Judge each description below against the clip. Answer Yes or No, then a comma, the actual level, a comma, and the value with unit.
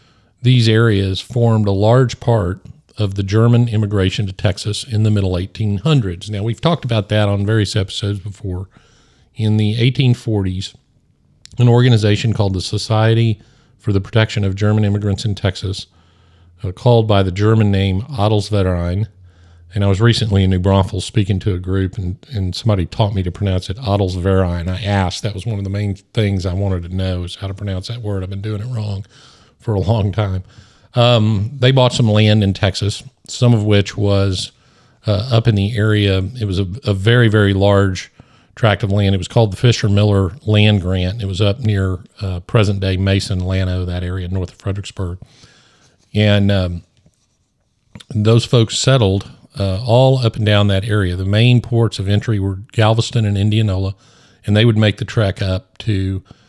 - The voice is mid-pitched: No, low, 105 Hz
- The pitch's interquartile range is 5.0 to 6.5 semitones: No, average, 2.8 semitones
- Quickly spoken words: No, average, 185 wpm